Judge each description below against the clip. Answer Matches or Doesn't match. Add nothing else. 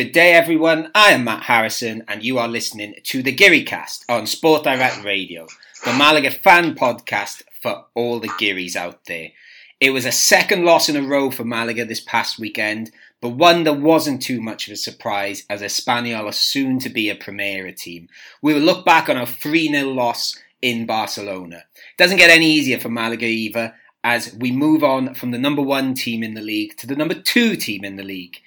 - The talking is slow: Doesn't match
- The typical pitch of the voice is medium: Doesn't match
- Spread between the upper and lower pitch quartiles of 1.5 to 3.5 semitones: Doesn't match